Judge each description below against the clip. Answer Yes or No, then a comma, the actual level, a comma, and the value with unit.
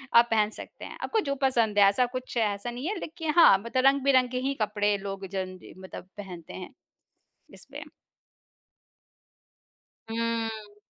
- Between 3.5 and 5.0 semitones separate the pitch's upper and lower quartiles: Yes, average, 4.1 semitones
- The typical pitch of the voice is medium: No, high, 225 Hz